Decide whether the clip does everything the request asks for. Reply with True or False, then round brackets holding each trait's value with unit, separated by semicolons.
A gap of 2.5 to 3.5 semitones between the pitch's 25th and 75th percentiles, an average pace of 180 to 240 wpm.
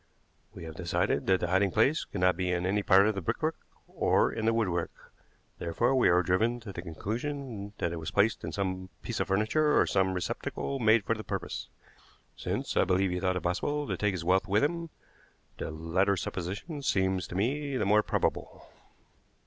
False (4.0 semitones; 200 wpm)